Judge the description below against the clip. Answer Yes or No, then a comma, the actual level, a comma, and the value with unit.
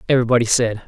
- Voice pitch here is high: No, low, 120 Hz